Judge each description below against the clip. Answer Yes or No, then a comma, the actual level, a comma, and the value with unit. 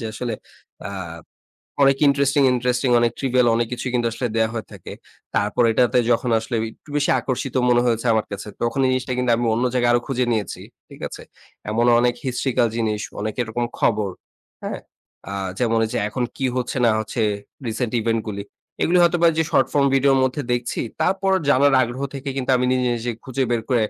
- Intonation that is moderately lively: No, narrow, 2.3 semitones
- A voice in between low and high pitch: No, low, 120 Hz